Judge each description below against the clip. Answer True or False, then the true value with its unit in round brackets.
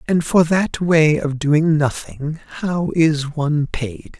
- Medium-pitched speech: True (150 Hz)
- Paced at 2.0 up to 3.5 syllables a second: True (3.3 syllables/s)